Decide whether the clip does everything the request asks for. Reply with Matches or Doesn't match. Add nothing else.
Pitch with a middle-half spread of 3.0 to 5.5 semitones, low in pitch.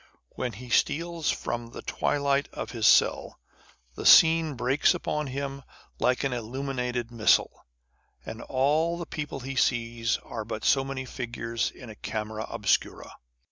Matches